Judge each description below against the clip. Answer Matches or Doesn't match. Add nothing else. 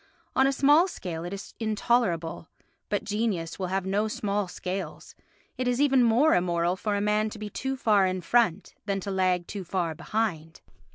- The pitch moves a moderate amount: Matches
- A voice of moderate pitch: Doesn't match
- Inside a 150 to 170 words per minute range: Doesn't match